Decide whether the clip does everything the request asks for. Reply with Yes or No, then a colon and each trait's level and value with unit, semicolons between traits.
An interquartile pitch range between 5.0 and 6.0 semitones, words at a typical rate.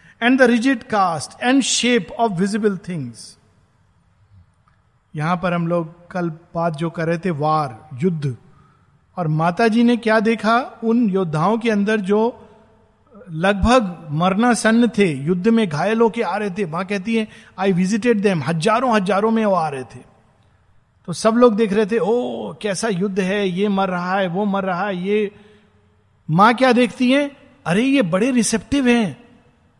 Yes: wide, 5.5 semitones; average, 170 wpm